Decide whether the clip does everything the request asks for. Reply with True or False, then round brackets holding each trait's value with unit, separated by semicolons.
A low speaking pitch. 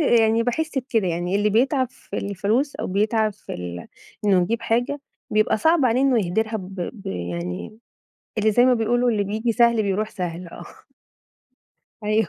False (220 Hz)